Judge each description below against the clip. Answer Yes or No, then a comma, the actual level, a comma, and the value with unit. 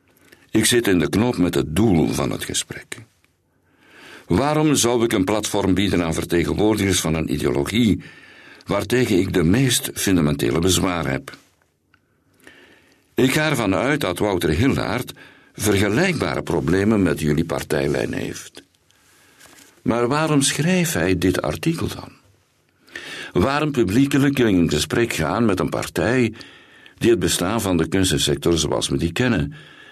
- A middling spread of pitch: No, wide, 6.5 semitones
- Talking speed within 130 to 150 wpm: Yes, slow, 135 wpm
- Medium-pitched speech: No, very low, 95 Hz